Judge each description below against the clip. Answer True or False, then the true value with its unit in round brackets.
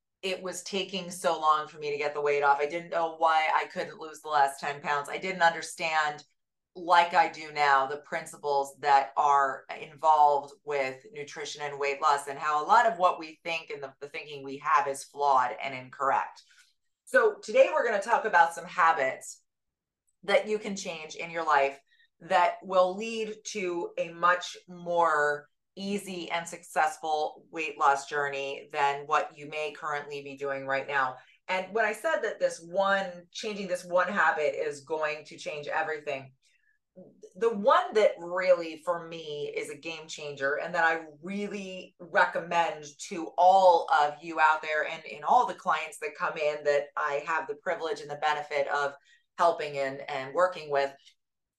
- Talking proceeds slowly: False (180 wpm)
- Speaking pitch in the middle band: True (160 Hz)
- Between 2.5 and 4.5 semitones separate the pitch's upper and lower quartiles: True (3.9 semitones)